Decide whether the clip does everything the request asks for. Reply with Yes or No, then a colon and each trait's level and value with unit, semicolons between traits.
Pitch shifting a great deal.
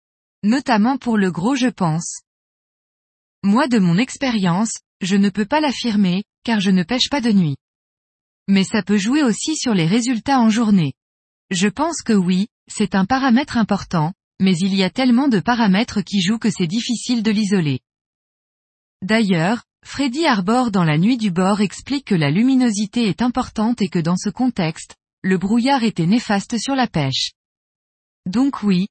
No: average, 4.4 semitones